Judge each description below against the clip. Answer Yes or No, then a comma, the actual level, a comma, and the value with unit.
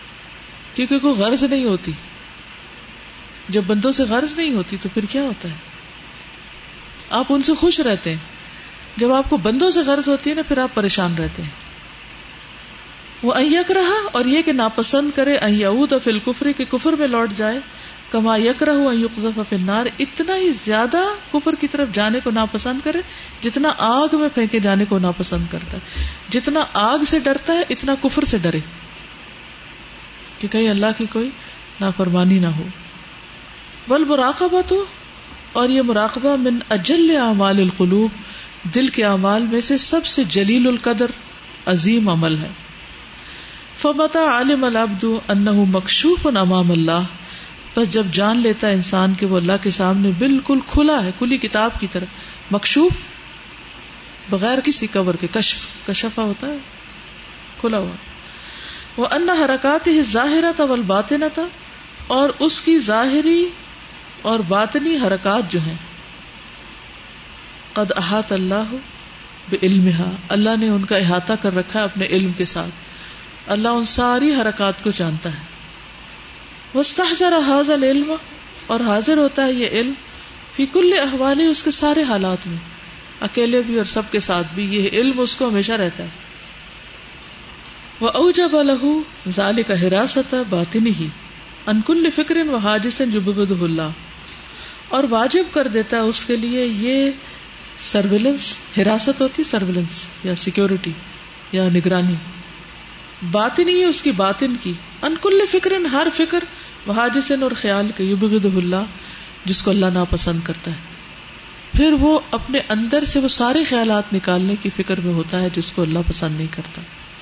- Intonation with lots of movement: Yes, wide, 6.4 semitones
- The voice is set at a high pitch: Yes, high, 225 Hz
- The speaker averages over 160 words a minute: No, average, 150 wpm